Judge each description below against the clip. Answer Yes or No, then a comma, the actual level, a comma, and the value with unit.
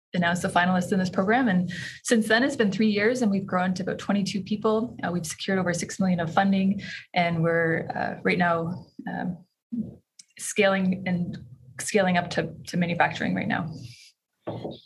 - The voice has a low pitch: No, medium, 185 Hz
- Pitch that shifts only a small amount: No, average, 3.0 semitones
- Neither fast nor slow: Yes, average, 175 wpm